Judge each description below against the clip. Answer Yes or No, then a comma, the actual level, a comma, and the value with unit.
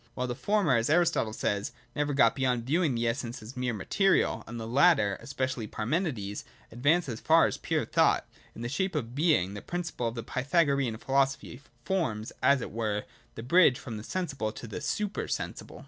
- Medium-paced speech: Yes, average, 195 wpm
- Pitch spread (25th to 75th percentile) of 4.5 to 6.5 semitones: Yes, average, 5.1 semitones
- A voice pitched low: Yes, low, 125 Hz